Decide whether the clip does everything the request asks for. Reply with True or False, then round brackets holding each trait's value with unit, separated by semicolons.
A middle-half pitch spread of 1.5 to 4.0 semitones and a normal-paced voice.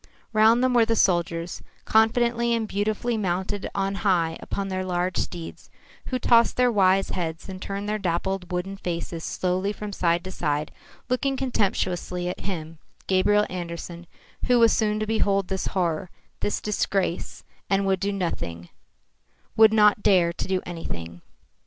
True (3.3 semitones; 155 wpm)